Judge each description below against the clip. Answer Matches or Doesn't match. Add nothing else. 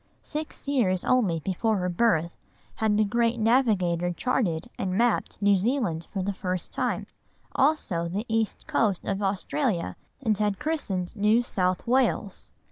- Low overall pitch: Doesn't match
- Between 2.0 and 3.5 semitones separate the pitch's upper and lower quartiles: Doesn't match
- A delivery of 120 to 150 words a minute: Matches